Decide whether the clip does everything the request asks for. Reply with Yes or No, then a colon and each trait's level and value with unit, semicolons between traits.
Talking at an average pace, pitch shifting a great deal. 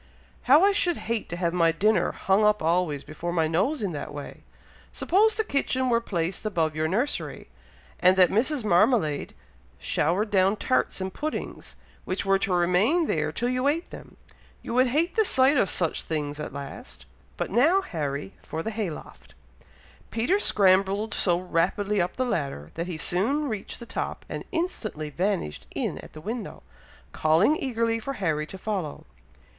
Yes: average, 175 wpm; wide, 6.8 semitones